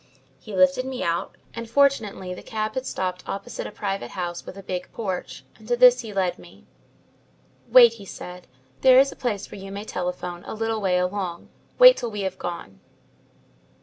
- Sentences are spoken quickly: No, average, 190 wpm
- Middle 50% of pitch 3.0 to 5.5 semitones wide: Yes, average, 4.2 semitones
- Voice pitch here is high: Yes, high, 195 Hz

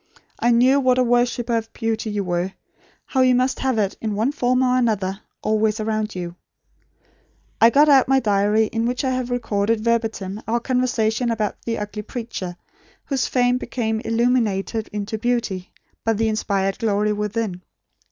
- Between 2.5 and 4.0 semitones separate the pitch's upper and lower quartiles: Yes, average, 2.8 semitones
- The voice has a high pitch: Yes, high, 225 Hz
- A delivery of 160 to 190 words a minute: Yes, average, 165 wpm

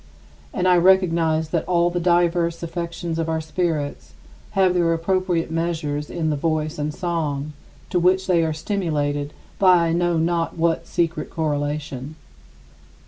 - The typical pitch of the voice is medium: Yes, medium, 165 Hz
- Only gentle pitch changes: Yes, narrow, 2.1 semitones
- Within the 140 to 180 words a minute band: Yes, average, 145 wpm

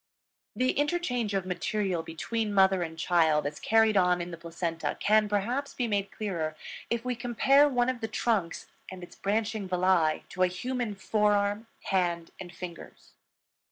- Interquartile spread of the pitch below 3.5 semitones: No, average, 4.3 semitones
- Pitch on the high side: Yes, high, 200 Hz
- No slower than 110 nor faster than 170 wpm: Yes, average, 160 wpm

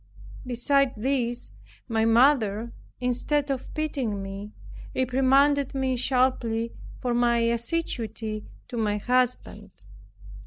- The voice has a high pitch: Yes, high, 245 Hz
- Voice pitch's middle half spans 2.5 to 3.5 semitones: Yes, average, 2.8 semitones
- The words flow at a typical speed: No, slow, 95 wpm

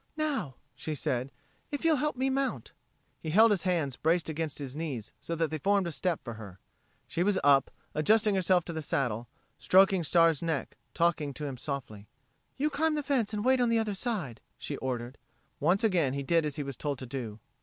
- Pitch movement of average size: No, wide, 7.0 semitones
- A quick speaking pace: Yes, fast, 210 wpm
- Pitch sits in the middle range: Yes, medium, 165 Hz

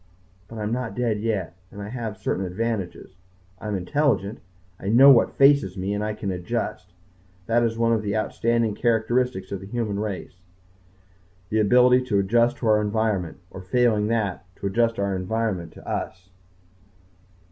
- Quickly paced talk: No, average, 170 wpm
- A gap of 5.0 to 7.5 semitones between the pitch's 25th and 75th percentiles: No, average, 3.2 semitones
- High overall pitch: No, low, 110 Hz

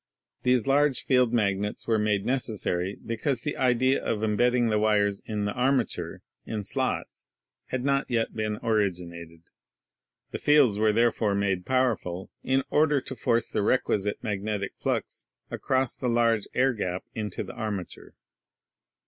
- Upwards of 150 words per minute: No, average, 145 wpm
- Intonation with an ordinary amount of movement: Yes, average, 3.7 semitones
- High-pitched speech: No, low, 110 Hz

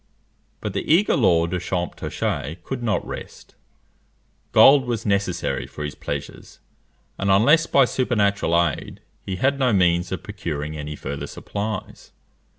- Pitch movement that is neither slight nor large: No, wide, 6.1 semitones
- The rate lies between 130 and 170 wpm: Yes, average, 140 wpm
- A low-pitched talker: Yes, low, 100 Hz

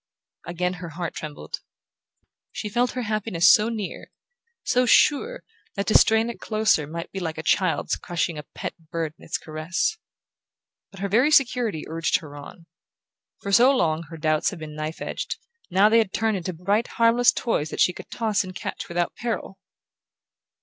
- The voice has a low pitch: No, high, 190 Hz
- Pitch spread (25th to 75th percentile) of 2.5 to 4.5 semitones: No, wide, 5.5 semitones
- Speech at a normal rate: Yes, average, 175 wpm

